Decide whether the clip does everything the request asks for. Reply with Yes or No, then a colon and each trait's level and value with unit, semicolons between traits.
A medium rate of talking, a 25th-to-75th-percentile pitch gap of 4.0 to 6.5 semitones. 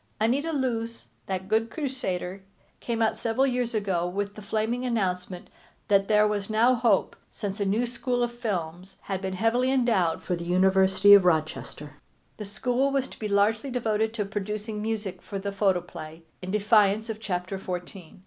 No: average, 170 wpm; average, 3.4 semitones